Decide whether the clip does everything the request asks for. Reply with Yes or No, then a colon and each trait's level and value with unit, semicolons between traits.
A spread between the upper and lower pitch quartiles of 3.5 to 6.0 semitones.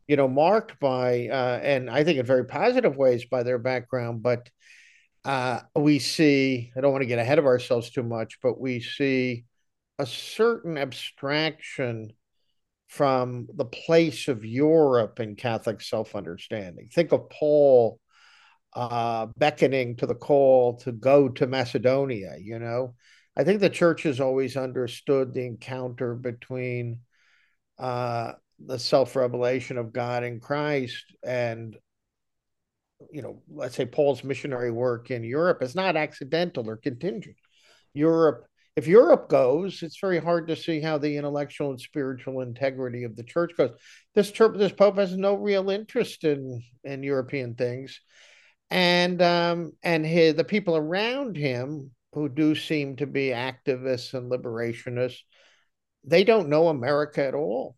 Yes: average, 4.0 semitones